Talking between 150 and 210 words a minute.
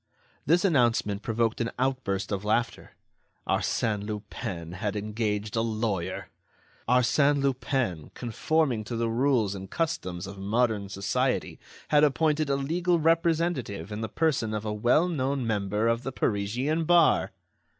No: average, 140 wpm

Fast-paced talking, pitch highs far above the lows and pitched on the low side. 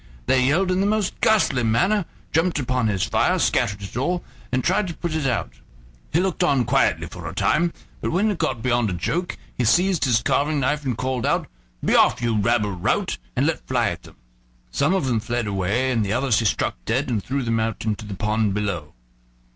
Yes: fast, 220 wpm; wide, 6.7 semitones; low, 125 Hz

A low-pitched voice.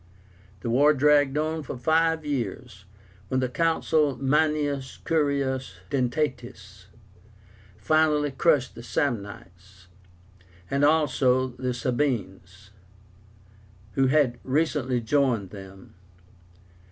Yes: low, 130 Hz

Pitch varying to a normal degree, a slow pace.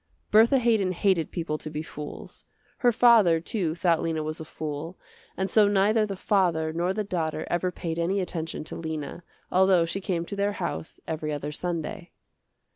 No: average, 3.8 semitones; average, 180 wpm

